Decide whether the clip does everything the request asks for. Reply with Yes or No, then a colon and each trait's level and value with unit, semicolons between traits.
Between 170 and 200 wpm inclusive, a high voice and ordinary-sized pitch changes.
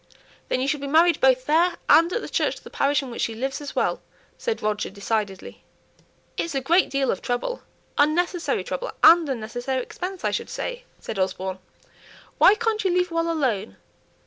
No: average, 190 wpm; very high, 285 Hz; wide, 6.4 semitones